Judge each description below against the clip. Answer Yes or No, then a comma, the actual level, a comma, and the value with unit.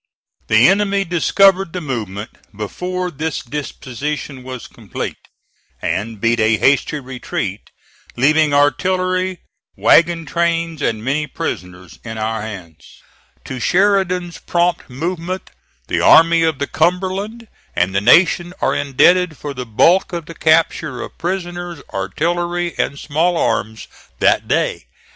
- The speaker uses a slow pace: Yes, slow, 125 wpm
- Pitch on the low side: No, medium, 160 Hz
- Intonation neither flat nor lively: No, wide, 5.9 semitones